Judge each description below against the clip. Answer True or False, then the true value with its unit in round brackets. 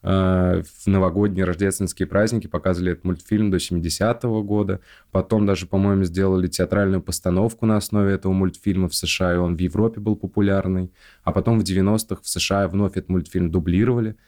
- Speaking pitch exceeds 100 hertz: False (95 Hz)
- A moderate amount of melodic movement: False (2.1 semitones)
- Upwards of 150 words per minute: True (160 wpm)